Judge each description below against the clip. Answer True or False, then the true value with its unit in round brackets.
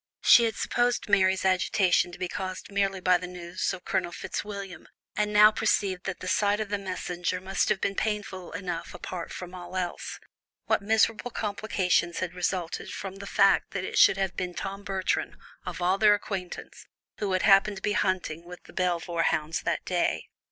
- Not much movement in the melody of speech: True (2.0 semitones)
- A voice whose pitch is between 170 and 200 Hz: True (190 Hz)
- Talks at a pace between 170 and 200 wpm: True (185 wpm)